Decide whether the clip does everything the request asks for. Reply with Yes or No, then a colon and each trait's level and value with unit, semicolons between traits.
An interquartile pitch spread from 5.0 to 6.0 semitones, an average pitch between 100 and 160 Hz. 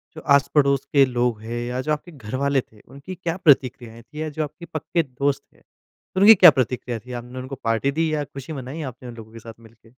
No: average, 3.7 semitones; low, 135 Hz